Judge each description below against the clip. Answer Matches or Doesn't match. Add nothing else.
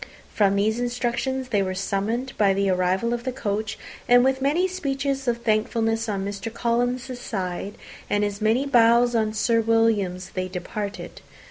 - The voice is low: Doesn't match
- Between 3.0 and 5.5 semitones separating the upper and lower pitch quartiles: Matches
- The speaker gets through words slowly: Doesn't match